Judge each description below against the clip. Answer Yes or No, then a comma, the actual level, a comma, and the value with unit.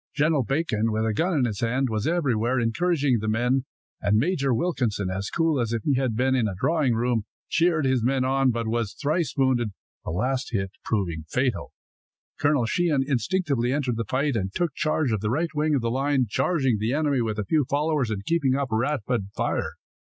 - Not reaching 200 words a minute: No, fast, 205 wpm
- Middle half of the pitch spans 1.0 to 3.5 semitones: No, average, 4.6 semitones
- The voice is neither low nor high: No, low, 130 Hz